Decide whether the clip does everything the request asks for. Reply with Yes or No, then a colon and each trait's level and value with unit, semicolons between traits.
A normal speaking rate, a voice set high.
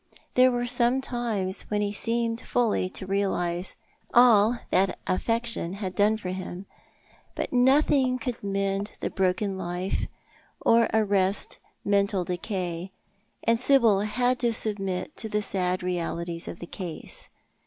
No: slow, 130 wpm; high, 205 Hz